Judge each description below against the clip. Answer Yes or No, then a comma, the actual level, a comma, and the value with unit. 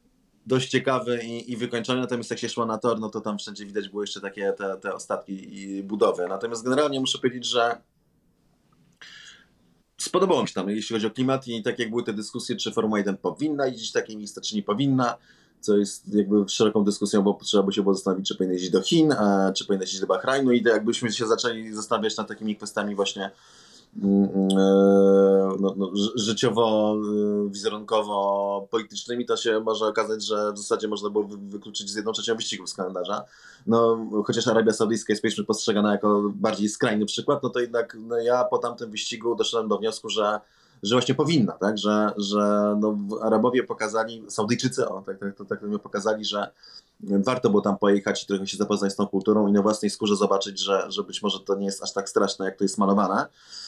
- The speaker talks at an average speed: No, fast, 195 wpm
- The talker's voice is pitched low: Yes, low, 105 Hz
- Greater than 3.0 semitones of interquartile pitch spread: No, narrow, 2.5 semitones